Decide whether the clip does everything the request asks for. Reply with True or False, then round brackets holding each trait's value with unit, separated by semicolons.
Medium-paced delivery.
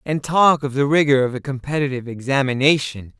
True (170 wpm)